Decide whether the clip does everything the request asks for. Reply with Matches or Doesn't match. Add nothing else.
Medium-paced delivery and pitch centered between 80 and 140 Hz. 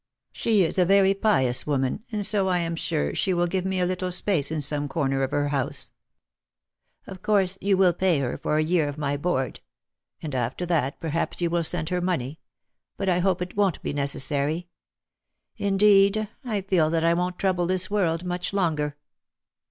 Doesn't match